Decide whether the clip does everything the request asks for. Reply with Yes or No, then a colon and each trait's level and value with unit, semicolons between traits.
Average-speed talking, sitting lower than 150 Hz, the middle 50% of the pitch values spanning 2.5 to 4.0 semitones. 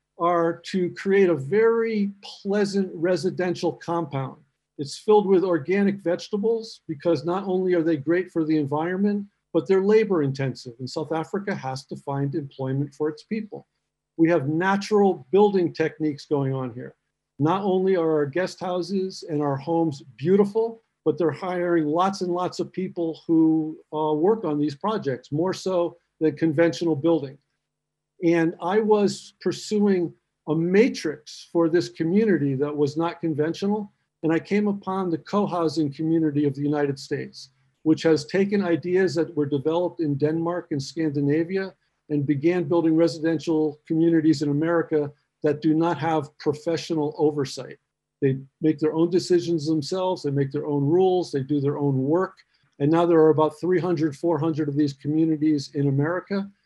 No: average, 160 wpm; medium, 165 Hz; average, 3.4 semitones